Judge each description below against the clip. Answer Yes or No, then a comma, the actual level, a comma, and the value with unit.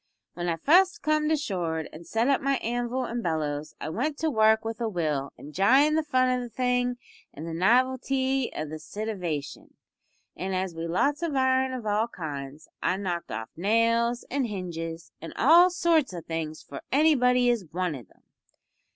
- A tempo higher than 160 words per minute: Yes, average, 175 wpm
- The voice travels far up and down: Yes, wide, 7.8 semitones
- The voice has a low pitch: No, high, 225 Hz